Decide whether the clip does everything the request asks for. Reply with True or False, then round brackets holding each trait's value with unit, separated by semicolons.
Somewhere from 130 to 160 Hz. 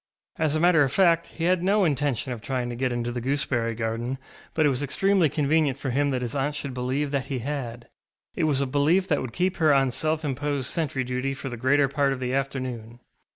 True (135 Hz)